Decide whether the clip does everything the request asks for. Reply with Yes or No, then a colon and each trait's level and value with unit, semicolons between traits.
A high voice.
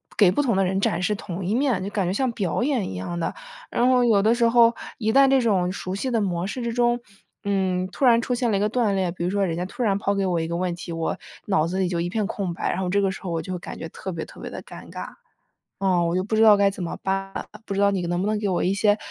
Yes: high, 195 Hz